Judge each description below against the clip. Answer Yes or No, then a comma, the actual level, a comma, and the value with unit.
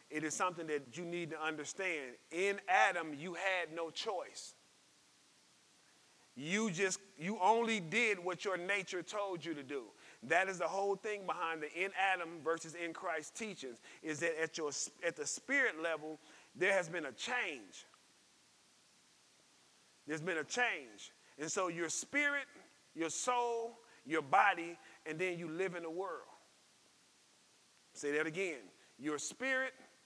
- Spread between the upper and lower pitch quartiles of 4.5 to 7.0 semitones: No, average, 3.9 semitones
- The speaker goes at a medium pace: Yes, average, 150 wpm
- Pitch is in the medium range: Yes, medium, 175 Hz